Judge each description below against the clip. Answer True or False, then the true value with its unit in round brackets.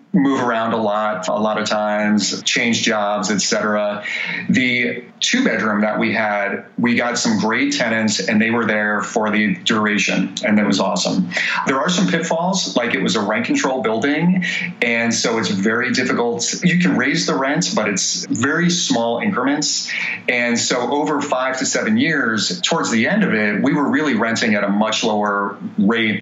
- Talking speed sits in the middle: True (185 wpm)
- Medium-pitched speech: False (115 Hz)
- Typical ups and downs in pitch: False (6.2 semitones)